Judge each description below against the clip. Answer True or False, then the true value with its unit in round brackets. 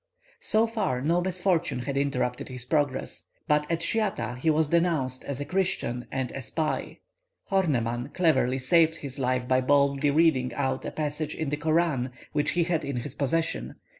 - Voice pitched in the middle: True (145 Hz)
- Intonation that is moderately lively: True (4.3 semitones)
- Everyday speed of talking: True (170 wpm)